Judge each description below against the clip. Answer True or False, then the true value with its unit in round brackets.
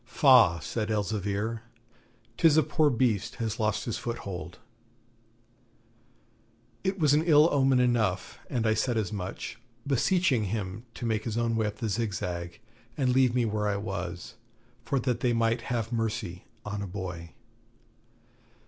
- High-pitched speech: False (115 Hz)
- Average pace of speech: True (150 wpm)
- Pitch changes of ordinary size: True (3.6 semitones)